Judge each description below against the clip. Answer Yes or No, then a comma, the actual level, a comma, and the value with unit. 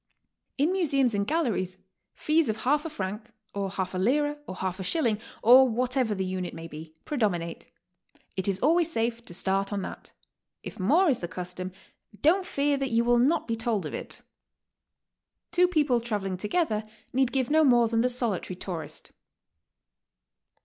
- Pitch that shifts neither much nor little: No, wide, 6.8 semitones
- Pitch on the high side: Yes, high, 230 Hz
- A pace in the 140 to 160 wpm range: No, average, 175 wpm